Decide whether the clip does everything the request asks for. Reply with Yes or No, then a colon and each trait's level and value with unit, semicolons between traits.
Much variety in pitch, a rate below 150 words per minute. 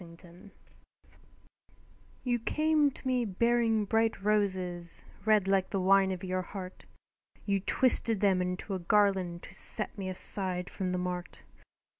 No: average, 3.2 semitones; average, 140 wpm